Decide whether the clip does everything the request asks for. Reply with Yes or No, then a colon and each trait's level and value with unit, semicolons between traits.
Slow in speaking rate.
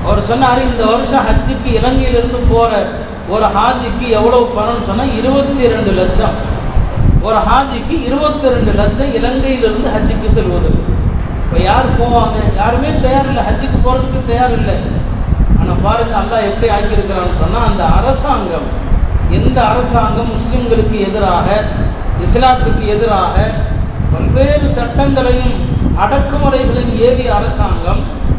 No: average, 110 wpm